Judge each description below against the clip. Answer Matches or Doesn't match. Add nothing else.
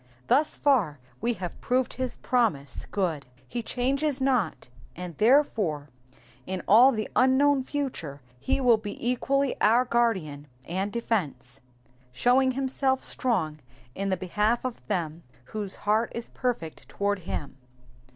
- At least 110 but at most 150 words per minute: Matches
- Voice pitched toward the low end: Doesn't match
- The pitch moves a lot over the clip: Matches